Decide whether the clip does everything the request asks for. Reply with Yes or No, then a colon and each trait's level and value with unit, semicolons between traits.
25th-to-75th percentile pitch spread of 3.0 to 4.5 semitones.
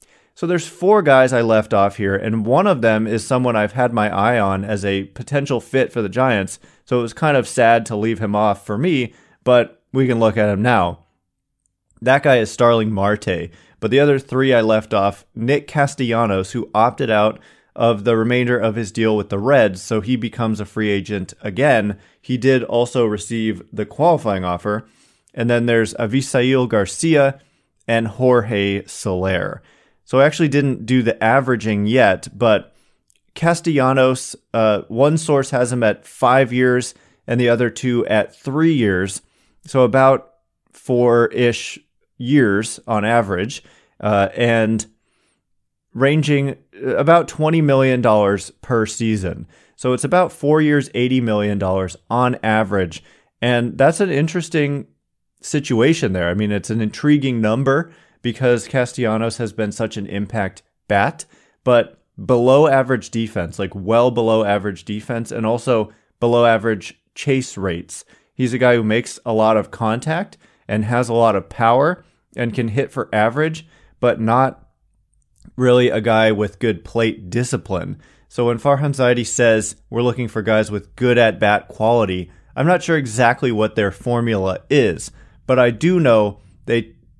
Yes: average, 3.5 semitones